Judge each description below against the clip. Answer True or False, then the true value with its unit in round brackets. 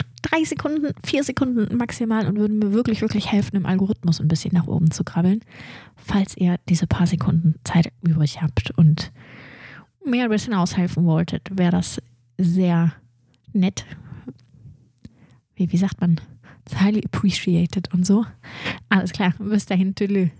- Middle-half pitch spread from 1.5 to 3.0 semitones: False (4.3 semitones)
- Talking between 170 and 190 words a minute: False (145 wpm)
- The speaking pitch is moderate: True (180 Hz)